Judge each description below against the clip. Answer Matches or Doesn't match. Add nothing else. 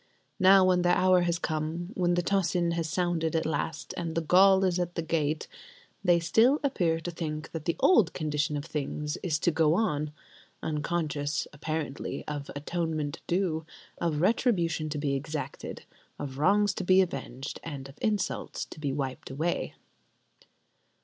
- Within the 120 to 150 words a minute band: Doesn't match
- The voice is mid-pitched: Matches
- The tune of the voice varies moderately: Matches